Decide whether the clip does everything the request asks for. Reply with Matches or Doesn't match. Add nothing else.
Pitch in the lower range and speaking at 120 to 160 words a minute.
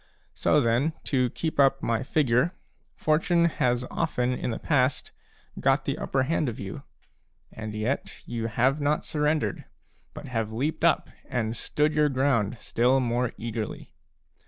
Matches